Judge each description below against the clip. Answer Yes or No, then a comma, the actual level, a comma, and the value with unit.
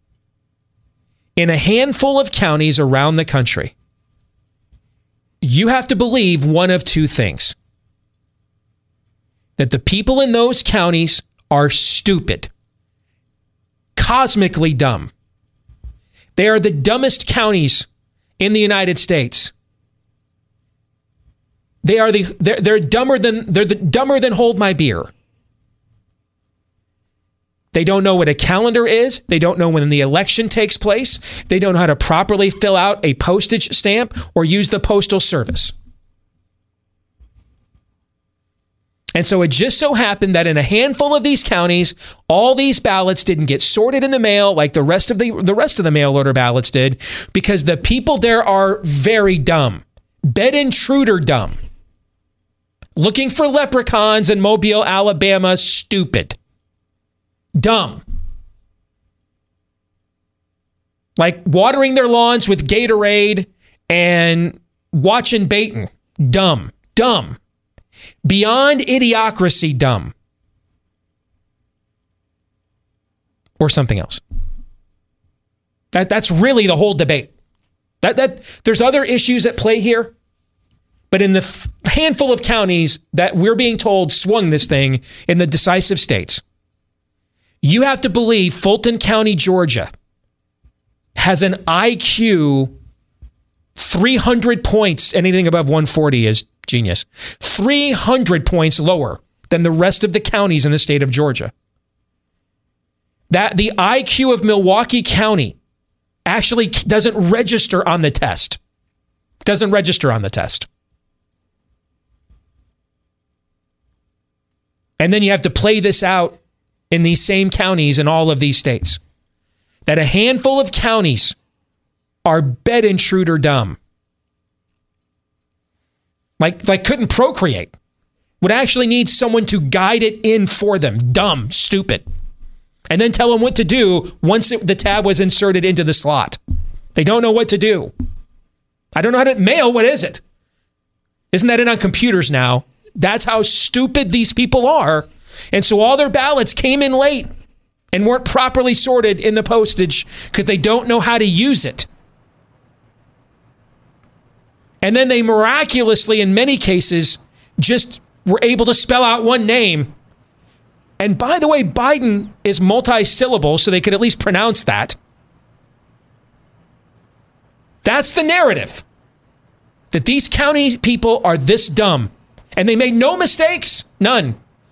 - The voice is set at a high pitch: No, medium, 175 Hz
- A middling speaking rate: No, slow, 130 wpm